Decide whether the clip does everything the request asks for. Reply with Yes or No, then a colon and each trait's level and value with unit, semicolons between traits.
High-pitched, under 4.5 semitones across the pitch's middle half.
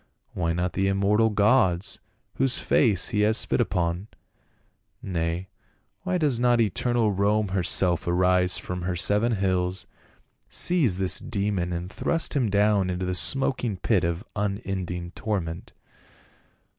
No: very low, 95 Hz; average, 3.2 semitones